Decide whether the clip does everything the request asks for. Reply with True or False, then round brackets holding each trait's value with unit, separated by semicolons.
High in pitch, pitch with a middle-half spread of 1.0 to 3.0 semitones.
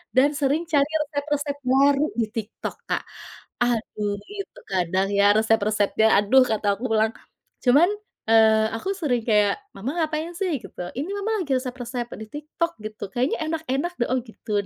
False (250 Hz; 5.2 semitones)